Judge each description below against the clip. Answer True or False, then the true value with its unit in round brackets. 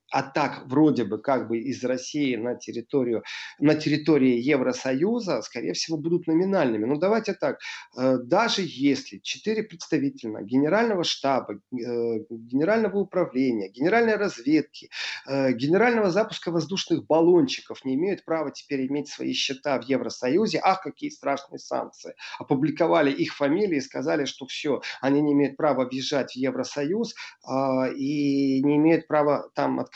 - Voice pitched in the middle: True (145 Hz)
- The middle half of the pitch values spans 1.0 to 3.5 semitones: False (4.4 semitones)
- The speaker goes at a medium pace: True (135 wpm)